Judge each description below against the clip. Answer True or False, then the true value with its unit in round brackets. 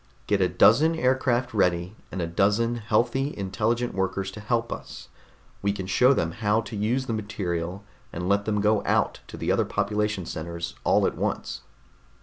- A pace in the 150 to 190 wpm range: True (175 wpm)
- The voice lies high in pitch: False (105 Hz)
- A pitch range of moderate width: True (3.7 semitones)